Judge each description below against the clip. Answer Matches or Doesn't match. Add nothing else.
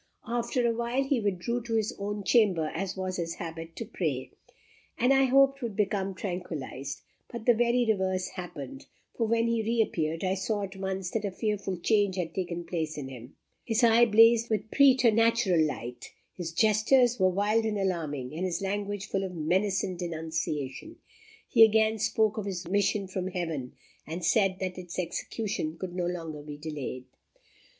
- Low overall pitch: Doesn't match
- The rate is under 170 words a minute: Doesn't match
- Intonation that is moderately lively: Matches